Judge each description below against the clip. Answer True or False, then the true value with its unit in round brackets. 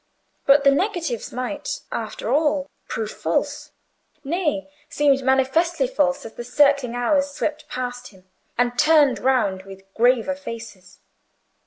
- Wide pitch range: False (3.4 semitones)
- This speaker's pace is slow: True (130 wpm)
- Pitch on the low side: False (270 Hz)